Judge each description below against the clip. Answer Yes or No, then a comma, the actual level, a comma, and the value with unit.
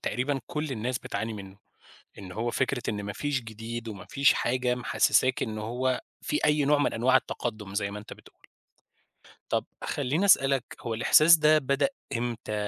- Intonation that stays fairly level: No, average, 4.0 semitones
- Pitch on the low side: Yes, low, 125 Hz